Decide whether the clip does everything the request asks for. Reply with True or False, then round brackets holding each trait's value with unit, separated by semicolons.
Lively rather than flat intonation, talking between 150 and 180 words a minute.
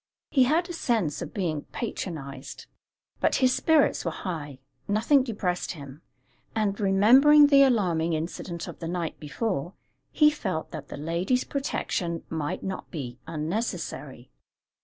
False (7.6 semitones; 140 wpm)